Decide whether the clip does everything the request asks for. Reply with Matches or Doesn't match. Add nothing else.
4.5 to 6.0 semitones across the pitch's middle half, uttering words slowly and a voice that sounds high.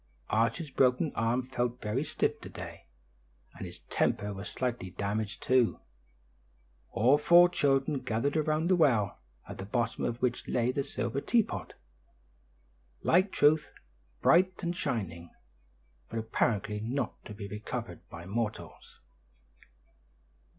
Doesn't match